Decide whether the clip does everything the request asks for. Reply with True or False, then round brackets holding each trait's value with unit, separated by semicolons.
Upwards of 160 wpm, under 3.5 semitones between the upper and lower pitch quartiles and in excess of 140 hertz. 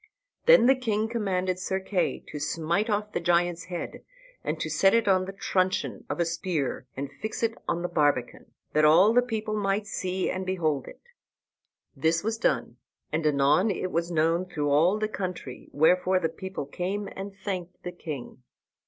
False (180 wpm; 3.8 semitones; 185 Hz)